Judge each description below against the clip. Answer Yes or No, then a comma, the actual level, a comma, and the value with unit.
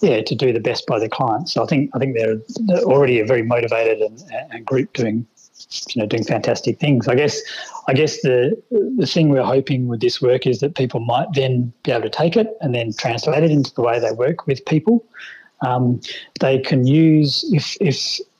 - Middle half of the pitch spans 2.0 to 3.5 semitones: No, average, 4.5 semitones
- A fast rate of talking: Yes, fast, 220 wpm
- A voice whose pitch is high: No, low, 135 Hz